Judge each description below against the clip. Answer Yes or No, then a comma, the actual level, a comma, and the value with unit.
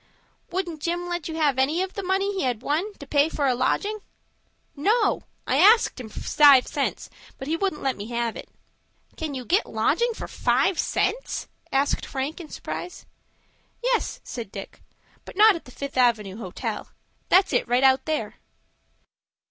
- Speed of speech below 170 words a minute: No, average, 175 wpm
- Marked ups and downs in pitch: Yes, wide, 6.5 semitones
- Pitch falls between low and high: No, very high, 300 Hz